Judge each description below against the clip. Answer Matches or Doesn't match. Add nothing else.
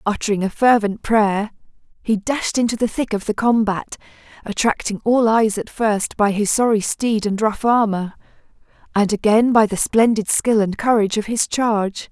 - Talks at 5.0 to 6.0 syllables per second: Doesn't match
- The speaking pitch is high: Matches